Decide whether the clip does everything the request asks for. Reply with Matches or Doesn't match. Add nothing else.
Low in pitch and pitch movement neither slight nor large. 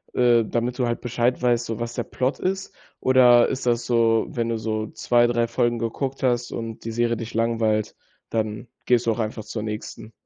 Doesn't match